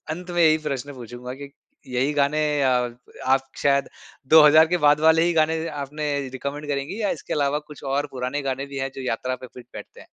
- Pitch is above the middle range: No, medium, 140 Hz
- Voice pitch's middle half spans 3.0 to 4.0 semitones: No, narrow, 2.4 semitones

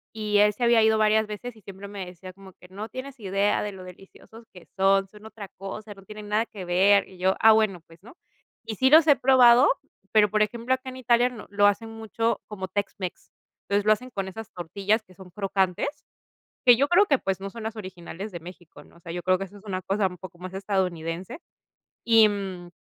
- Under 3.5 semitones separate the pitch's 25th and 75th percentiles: Yes, average, 2.9 semitones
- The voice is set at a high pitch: Yes, high, 205 Hz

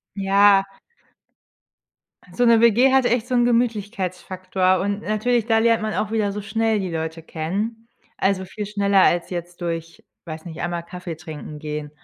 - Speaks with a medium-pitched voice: No, high, 200 Hz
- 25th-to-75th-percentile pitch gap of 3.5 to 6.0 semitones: Yes, average, 4.4 semitones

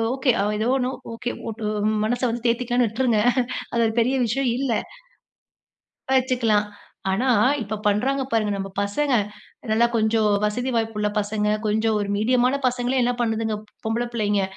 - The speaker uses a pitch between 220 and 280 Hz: Yes, high, 230 Hz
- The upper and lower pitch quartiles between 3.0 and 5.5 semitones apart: No, narrow, 2.6 semitones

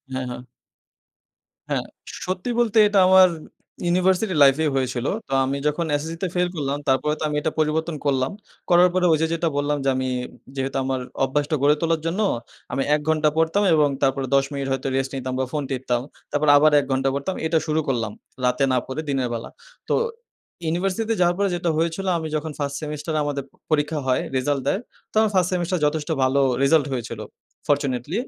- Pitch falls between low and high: Yes, medium, 150 Hz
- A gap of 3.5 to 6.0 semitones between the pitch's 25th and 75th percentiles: Yes, average, 4.0 semitones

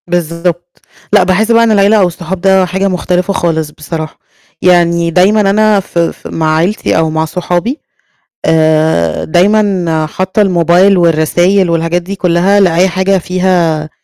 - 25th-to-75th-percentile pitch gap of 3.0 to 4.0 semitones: No, narrow, 2.5 semitones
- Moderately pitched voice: Yes, medium, 175 Hz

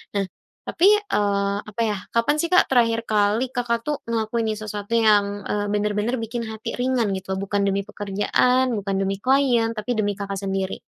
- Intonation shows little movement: No, average, 3.0 semitones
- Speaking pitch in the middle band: No, high, 215 Hz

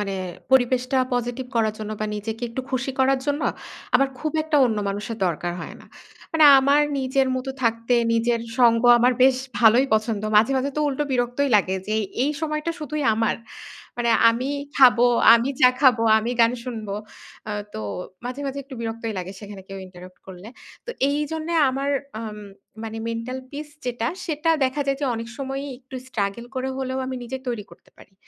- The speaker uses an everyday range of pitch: Yes, average, 3.2 semitones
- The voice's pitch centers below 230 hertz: No, high, 245 Hz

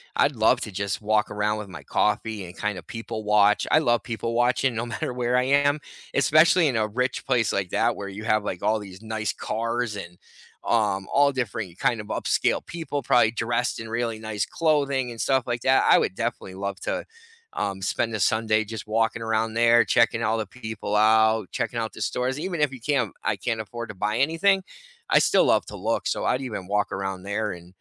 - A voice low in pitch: Yes, low, 110 Hz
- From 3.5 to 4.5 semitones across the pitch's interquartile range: No, average, 2.9 semitones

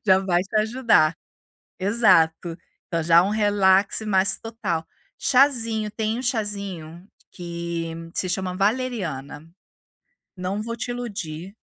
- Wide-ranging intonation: No, average, 4.4 semitones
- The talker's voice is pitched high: Yes, high, 195 Hz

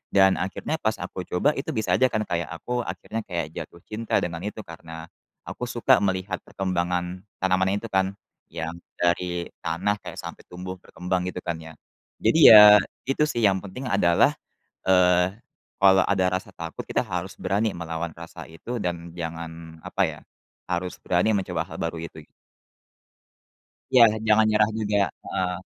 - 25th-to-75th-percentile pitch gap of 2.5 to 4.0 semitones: Yes, average, 2.9 semitones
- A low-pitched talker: Yes, very low, 90 Hz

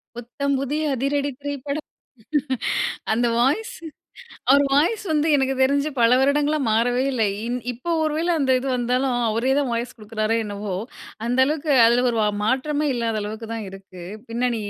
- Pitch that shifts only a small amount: No, average, 3.9 semitones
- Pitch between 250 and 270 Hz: Yes, very high, 255 Hz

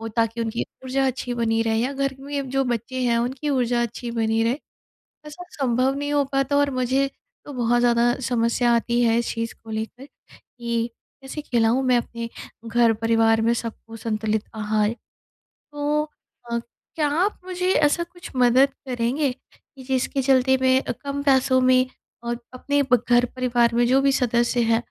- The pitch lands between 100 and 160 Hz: No, high, 245 Hz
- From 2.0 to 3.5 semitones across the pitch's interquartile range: Yes, narrow, 2.6 semitones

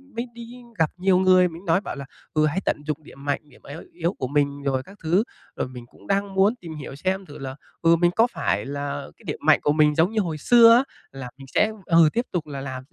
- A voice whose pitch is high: No, medium, 160 Hz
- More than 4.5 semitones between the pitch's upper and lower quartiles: Yes, average, 5.1 semitones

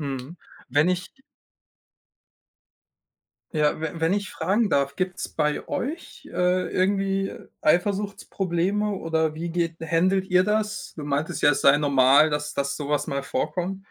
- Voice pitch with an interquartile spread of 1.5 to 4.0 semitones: No, average, 4.6 semitones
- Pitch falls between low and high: Yes, medium, 170 Hz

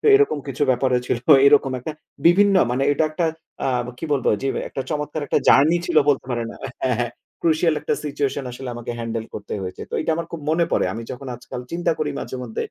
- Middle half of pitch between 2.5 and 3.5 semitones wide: No, average, 4.4 semitones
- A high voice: No, medium, 140 Hz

